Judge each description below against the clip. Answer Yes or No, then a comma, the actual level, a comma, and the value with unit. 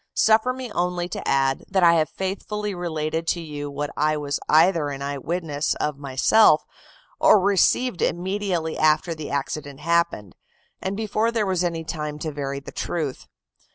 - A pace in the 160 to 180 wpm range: Yes, average, 165 wpm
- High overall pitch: No, medium, 165 Hz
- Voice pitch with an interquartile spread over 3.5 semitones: Yes, average, 4.4 semitones